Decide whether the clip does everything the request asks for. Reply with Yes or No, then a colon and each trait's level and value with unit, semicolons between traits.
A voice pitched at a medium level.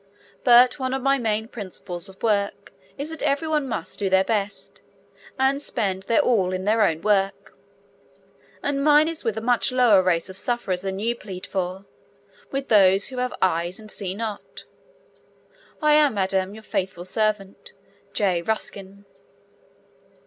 No: high, 210 Hz